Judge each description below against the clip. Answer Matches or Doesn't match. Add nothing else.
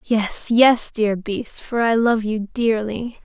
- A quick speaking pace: Doesn't match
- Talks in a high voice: Matches